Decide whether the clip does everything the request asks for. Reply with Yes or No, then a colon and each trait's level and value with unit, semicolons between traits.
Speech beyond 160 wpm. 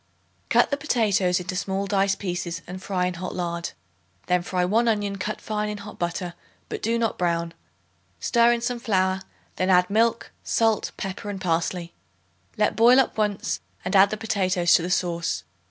Yes: average, 180 wpm